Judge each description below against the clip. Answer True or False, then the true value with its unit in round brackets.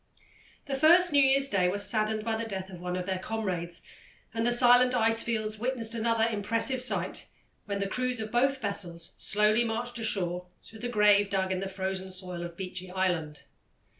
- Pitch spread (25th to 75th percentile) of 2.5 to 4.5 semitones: True (4.0 semitones)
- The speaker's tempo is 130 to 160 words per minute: False (190 wpm)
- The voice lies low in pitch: False (215 Hz)